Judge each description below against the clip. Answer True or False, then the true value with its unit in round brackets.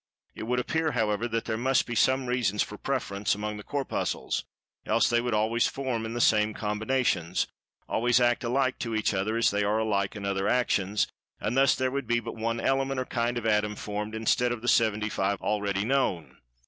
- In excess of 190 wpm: True (200 wpm)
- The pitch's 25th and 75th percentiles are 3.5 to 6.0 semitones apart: False (2.8 semitones)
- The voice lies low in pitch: True (115 Hz)